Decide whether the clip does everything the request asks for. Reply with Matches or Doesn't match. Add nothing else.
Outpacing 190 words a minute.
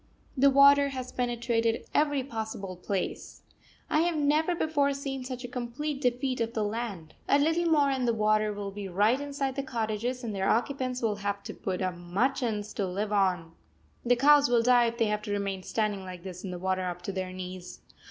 Matches